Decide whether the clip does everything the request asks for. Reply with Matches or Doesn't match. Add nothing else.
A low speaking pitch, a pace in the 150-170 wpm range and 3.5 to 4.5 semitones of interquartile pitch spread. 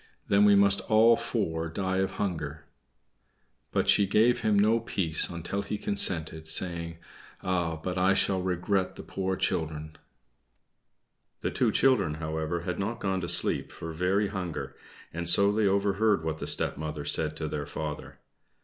Matches